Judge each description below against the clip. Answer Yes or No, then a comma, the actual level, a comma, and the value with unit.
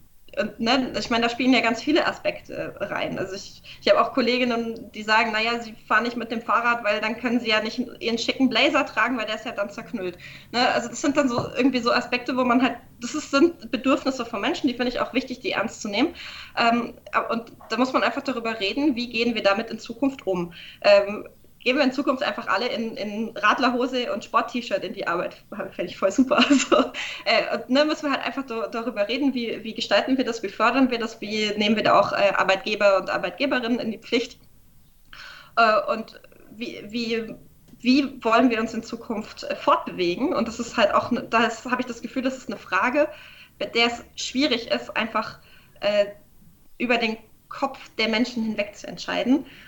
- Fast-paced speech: Yes, fast, 215 wpm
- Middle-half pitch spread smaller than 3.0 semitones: No, average, 3.3 semitones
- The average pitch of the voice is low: No, high, 240 Hz